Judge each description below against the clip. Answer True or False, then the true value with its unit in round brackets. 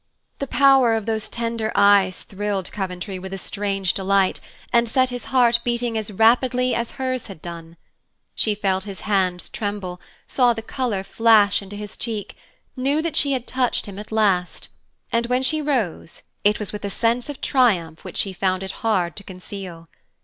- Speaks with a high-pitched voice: True (210 Hz)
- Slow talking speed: False (180 wpm)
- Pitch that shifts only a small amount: False (3.8 semitones)